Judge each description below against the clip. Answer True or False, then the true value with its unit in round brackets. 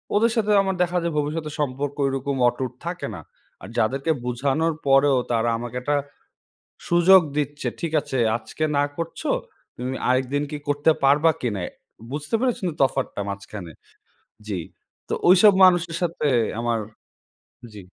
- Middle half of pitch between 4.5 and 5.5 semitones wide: True (4.8 semitones)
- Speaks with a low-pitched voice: False (145 Hz)